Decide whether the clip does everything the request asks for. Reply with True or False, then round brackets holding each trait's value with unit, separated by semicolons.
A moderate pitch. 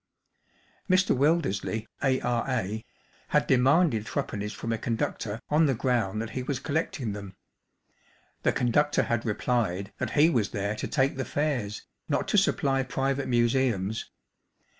False (120 Hz)